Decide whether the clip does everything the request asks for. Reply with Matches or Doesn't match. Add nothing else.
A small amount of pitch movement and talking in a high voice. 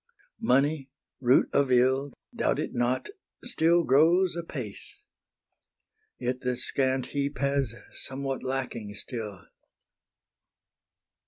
Doesn't match